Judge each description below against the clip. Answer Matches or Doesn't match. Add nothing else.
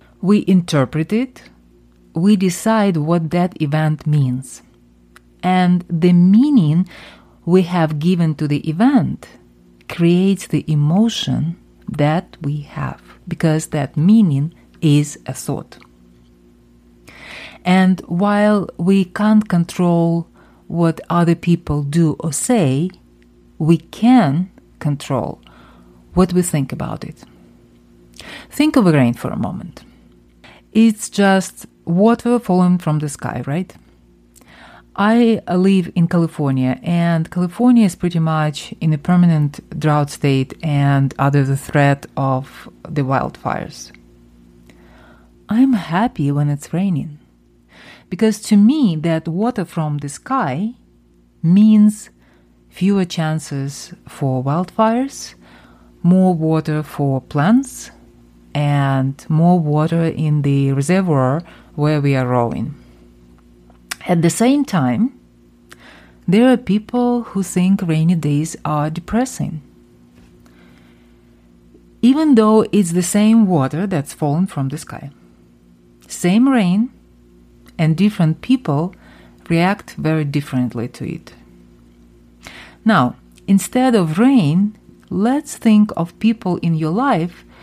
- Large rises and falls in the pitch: Matches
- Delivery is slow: Matches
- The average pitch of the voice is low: Doesn't match